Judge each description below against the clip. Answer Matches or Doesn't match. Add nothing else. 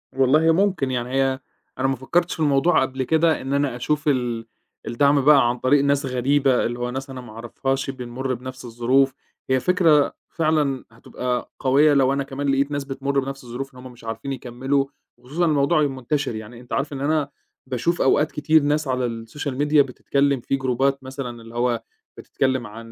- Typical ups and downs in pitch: Doesn't match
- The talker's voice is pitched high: Doesn't match